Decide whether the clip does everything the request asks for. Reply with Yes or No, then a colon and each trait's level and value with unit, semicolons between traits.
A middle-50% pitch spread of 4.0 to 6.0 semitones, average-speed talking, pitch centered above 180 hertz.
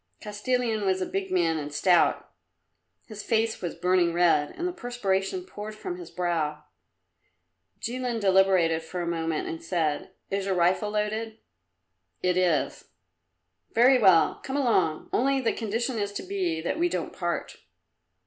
Yes: average, 4.6 semitones; average, 150 wpm; high, 190 Hz